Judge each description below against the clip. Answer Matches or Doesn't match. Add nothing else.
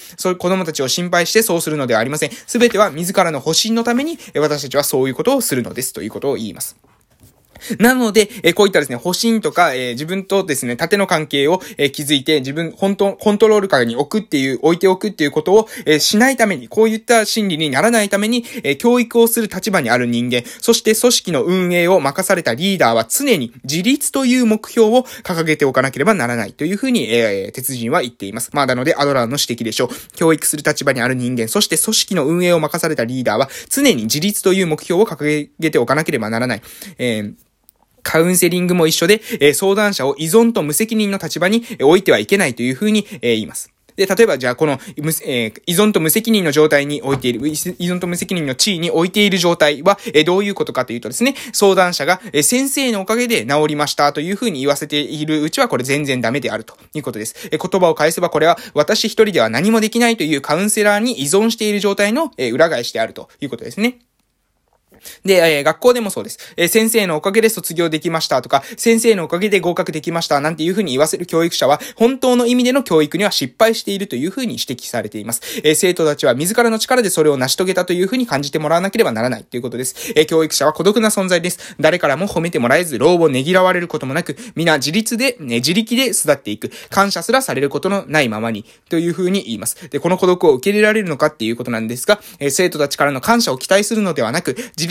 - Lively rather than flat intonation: Matches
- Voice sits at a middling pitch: Matches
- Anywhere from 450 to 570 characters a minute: Matches